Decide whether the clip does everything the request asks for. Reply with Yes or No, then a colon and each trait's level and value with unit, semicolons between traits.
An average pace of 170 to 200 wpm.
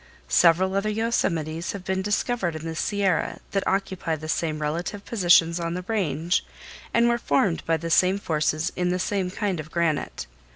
Yes: average, 175 wpm